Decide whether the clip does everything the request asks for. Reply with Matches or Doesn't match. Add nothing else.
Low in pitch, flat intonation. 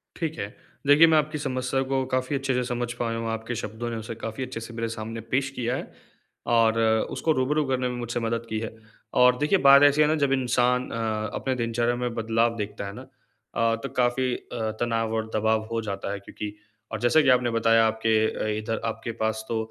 Matches